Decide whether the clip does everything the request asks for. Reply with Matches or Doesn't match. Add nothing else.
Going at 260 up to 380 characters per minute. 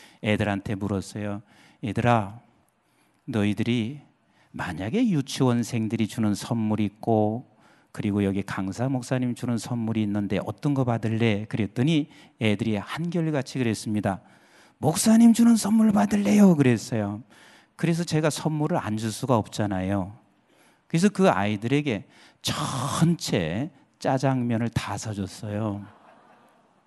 Matches